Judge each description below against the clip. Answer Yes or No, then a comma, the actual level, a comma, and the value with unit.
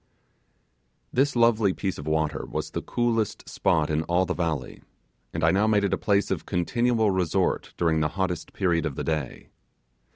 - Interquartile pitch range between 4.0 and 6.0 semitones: Yes, average, 4.9 semitones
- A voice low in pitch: Yes, very low, 90 Hz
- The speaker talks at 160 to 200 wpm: Yes, average, 175 wpm